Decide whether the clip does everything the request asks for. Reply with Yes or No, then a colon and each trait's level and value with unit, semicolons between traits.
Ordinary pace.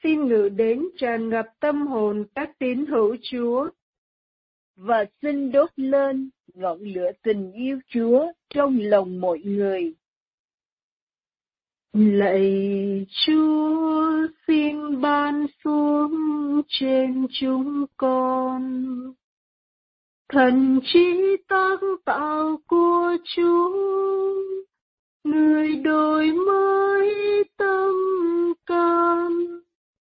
No: slow, 85 wpm